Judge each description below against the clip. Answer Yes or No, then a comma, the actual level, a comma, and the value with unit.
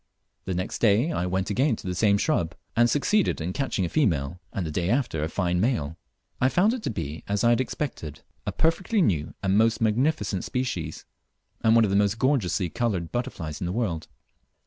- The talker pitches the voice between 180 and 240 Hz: No, low, 105 Hz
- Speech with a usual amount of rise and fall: No, wide, 6.4 semitones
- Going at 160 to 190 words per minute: No, fast, 205 wpm